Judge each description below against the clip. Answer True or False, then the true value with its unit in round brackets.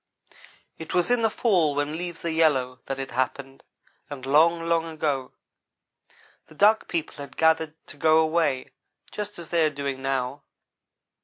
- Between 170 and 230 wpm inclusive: False (160 wpm)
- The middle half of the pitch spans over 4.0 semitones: False (3.5 semitones)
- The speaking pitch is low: False (155 Hz)